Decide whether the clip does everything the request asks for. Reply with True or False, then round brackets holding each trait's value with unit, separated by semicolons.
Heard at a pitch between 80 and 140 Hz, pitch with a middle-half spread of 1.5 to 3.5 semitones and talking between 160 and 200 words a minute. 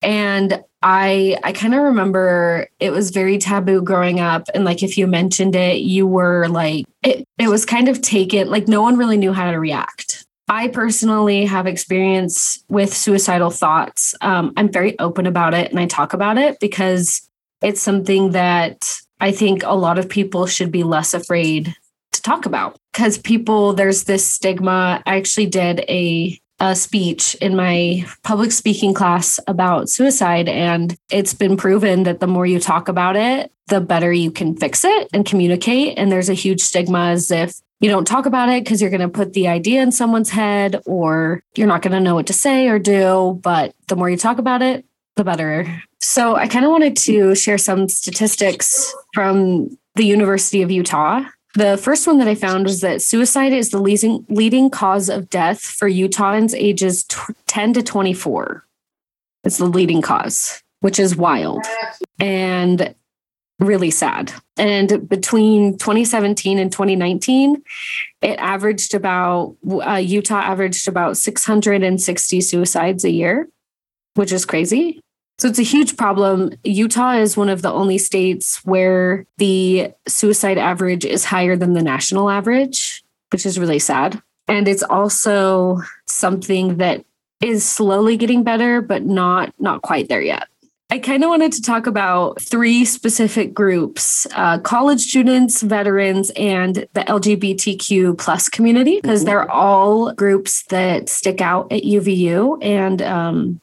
False (195 Hz; 2.9 semitones; 170 wpm)